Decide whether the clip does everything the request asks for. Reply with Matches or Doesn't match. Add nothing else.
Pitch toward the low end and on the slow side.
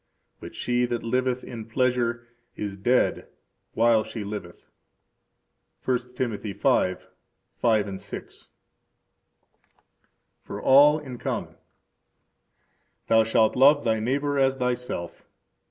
Matches